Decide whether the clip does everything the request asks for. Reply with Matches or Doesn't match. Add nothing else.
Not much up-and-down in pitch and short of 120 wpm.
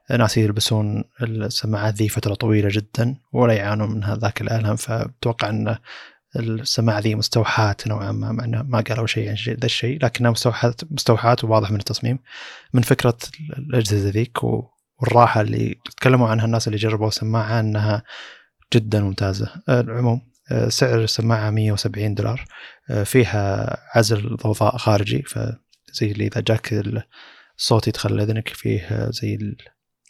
Doesn't match